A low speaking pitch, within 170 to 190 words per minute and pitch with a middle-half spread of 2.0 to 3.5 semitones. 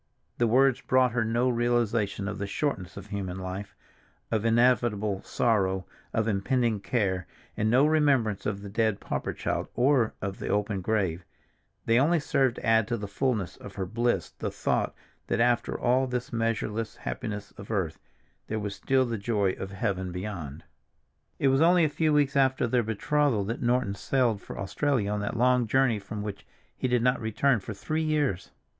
No: low, 115 Hz; average, 185 wpm; average, 4.0 semitones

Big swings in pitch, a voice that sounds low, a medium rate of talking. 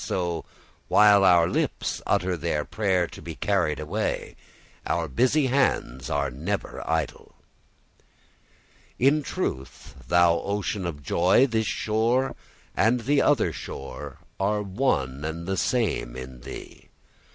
No: wide, 6.2 semitones; very low, 90 Hz; slow, 125 wpm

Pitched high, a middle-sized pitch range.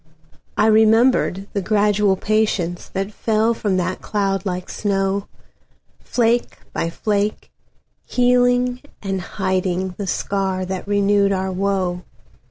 No: high, 200 Hz; narrow, 2.3 semitones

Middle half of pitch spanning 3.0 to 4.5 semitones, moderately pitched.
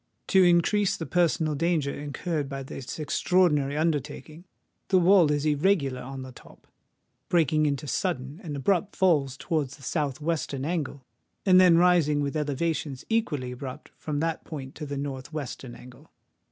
Yes: average, 3.5 semitones; medium, 150 Hz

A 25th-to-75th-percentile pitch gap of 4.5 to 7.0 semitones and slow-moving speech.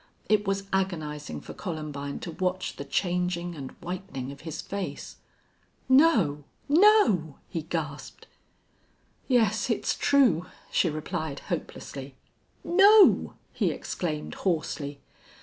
Yes: average, 5.1 semitones; slow, 110 wpm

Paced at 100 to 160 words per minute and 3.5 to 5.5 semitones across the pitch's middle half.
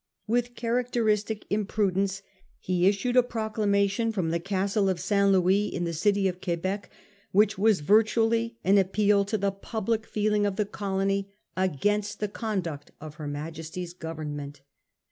No: average, 145 wpm; average, 2.7 semitones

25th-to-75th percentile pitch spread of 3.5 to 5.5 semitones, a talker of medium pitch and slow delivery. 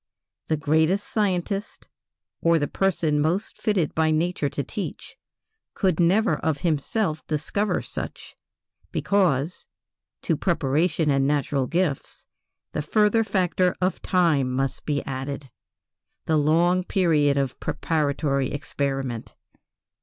Yes: average, 4.3 semitones; medium, 160 Hz; slow, 115 wpm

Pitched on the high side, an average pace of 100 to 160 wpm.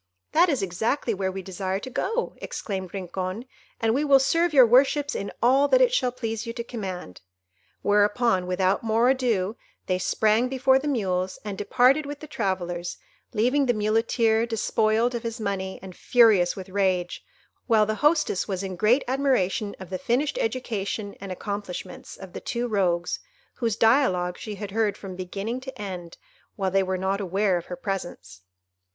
No: high, 210 Hz; average, 175 wpm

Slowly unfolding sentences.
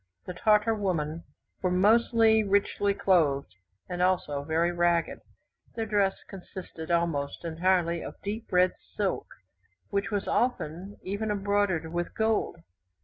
Yes: slow, 125 wpm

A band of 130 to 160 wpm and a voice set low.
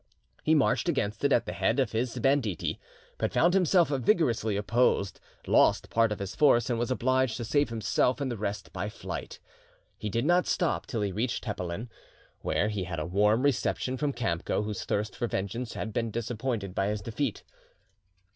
No: average, 185 wpm; low, 115 Hz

